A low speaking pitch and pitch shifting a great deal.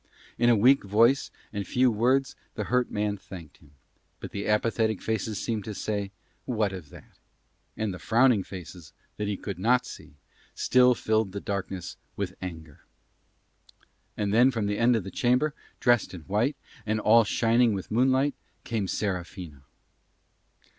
No: low, 105 Hz; average, 3.7 semitones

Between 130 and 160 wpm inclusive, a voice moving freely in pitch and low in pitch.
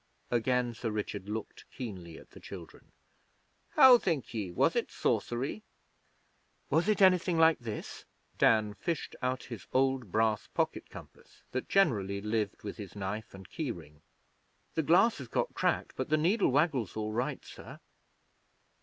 Yes: average, 155 wpm; wide, 7.0 semitones; low, 120 Hz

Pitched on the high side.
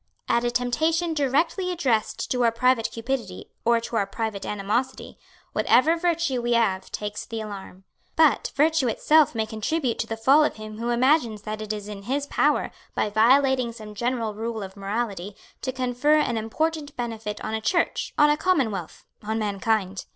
Yes: high, 235 Hz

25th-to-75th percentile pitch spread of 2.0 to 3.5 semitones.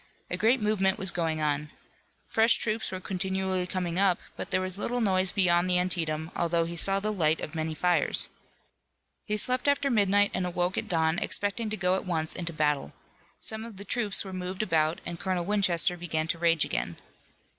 Yes: average, 3.2 semitones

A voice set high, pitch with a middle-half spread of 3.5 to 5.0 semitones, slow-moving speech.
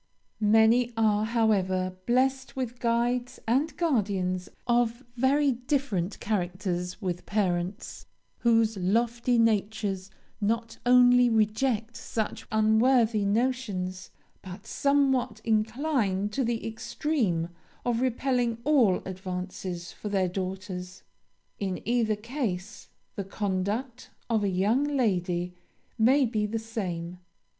Yes: high, 220 Hz; average, 4.4 semitones; slow, 105 wpm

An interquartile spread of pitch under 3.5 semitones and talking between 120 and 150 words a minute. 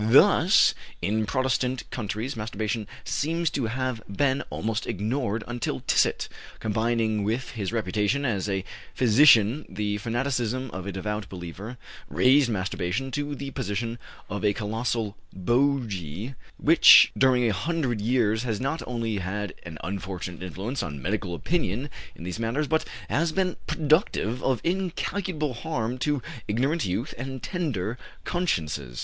No: average, 4.6 semitones; slow, 135 wpm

